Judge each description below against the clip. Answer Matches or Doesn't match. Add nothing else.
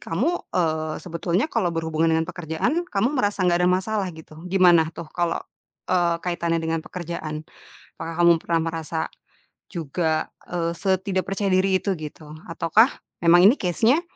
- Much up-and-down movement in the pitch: Doesn't match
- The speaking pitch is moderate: Matches